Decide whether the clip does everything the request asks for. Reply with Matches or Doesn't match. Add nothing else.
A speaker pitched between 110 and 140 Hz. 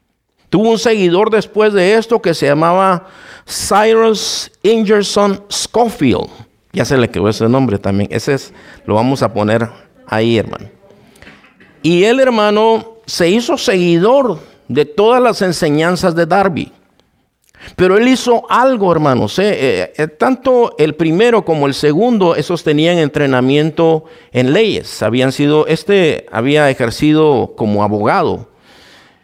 Doesn't match